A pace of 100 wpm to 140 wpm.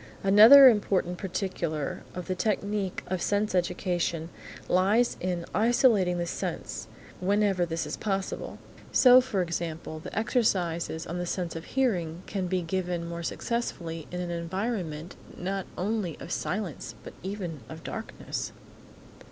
Yes: slow, 135 wpm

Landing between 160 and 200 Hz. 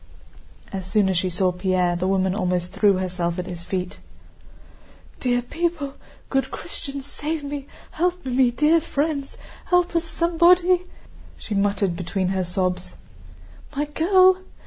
No: high, 240 Hz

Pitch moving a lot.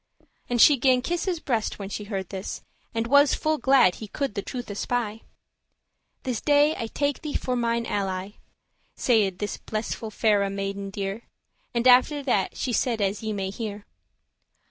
No: average, 4.3 semitones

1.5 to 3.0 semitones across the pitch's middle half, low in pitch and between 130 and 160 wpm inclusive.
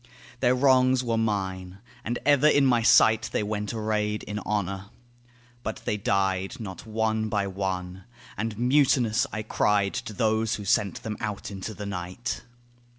Yes: narrow, 2.6 semitones; low, 105 Hz; average, 155 wpm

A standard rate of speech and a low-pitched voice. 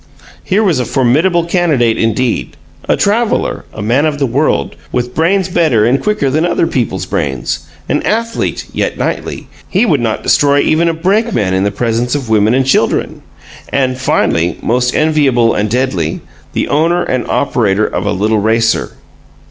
Yes: average, 165 wpm; low, 130 Hz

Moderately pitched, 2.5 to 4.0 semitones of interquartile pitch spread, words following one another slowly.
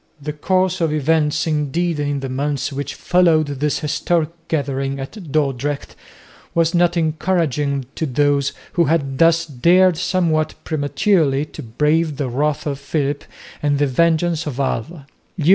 No: medium, 150 Hz; average, 2.9 semitones; average, 145 wpm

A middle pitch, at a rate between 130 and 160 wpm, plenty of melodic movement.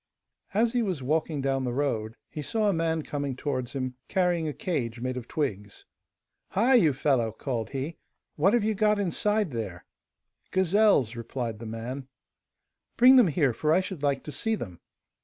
No: medium, 145 Hz; average, 175 wpm; wide, 7.1 semitones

